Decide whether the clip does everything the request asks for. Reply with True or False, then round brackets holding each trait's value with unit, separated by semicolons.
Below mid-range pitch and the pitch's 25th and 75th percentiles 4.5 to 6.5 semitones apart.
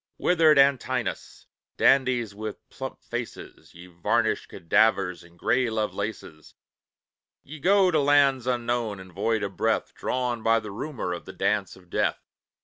True (115 Hz; 5.1 semitones)